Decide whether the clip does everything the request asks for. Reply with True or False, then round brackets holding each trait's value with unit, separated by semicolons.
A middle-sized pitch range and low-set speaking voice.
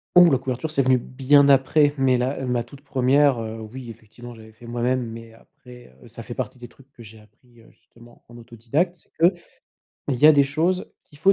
True (3.3 semitones; 125 Hz)